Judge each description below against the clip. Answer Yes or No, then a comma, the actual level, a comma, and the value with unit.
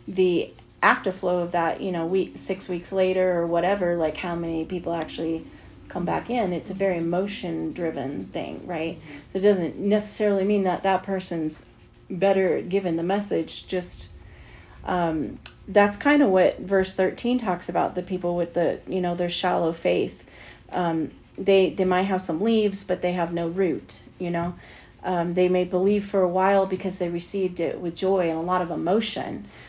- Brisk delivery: No, average, 180 wpm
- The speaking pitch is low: No, medium, 180 Hz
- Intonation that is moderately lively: No, narrow, 2.2 semitones